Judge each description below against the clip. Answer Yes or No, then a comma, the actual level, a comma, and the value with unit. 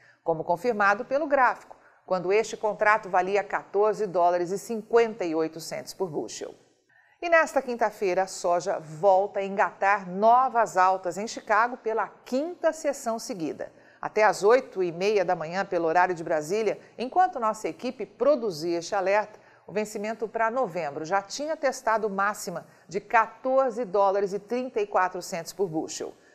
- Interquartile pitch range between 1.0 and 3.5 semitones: No, average, 4.1 semitones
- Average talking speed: Yes, average, 130 wpm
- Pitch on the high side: Yes, high, 210 Hz